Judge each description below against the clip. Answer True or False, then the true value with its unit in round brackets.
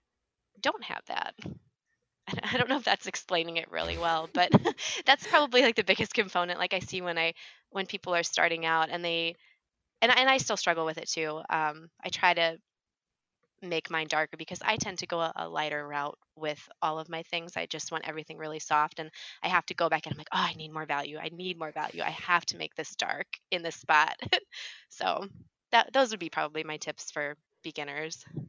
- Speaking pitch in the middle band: True (165 Hz)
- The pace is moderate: False (215 wpm)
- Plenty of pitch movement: False (2.5 semitones)